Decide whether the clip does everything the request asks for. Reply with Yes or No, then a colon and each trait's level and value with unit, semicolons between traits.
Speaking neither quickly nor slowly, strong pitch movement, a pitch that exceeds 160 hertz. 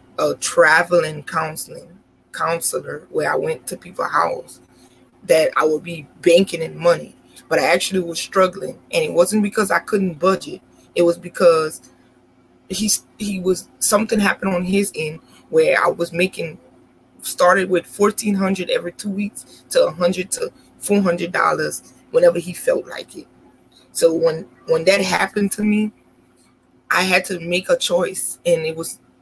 No: average, 160 wpm; average, 3.5 semitones; medium, 185 Hz